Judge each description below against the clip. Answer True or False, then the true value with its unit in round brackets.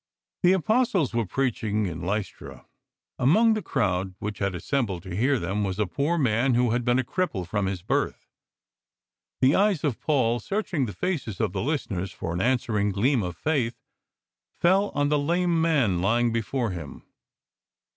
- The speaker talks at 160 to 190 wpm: True (170 wpm)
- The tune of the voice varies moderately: False (7.0 semitones)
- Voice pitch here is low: True (120 Hz)